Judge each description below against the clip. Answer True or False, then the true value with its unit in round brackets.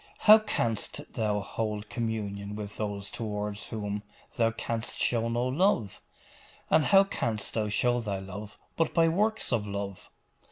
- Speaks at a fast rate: False (150 wpm)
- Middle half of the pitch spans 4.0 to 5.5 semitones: False (3.1 semitones)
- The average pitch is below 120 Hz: True (110 Hz)